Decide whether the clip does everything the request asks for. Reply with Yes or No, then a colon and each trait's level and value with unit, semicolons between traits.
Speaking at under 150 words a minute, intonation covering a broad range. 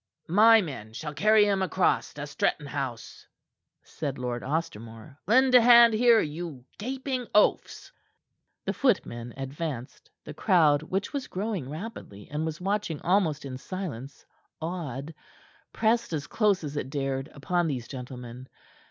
Yes: average, 140 wpm; wide, 7.4 semitones